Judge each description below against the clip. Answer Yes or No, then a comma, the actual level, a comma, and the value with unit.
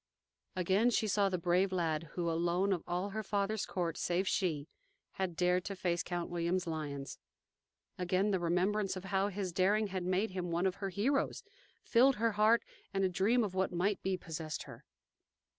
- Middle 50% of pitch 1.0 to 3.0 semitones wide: Yes, narrow, 2.4 semitones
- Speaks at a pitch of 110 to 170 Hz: No, medium, 185 Hz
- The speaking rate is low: No, average, 185 wpm